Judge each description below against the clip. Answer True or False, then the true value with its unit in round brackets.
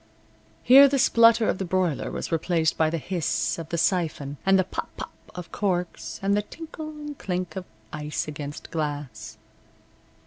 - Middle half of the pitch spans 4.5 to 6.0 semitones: True (5.0 semitones)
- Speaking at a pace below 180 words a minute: True (170 wpm)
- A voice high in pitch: False (175 Hz)